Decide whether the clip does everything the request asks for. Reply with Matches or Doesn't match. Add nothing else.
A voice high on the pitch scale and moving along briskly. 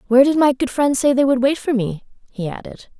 Matches